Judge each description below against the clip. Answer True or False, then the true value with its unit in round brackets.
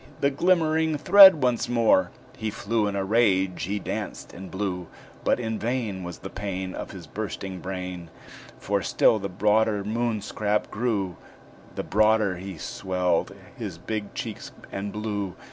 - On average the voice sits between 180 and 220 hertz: False (105 Hz)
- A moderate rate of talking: True (160 wpm)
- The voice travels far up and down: False (3.2 semitones)